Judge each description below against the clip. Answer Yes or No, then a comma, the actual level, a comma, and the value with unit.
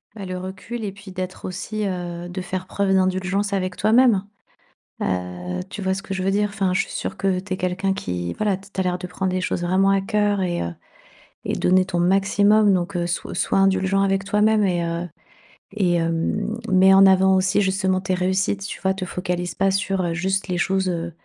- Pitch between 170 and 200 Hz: Yes, high, 190 Hz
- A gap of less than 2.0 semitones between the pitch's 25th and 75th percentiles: Yes, narrow, 1.4 semitones